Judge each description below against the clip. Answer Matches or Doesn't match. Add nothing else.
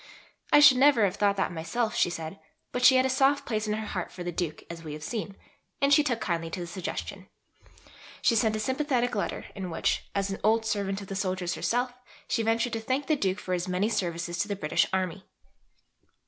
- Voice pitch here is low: Doesn't match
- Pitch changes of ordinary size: Matches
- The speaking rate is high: Matches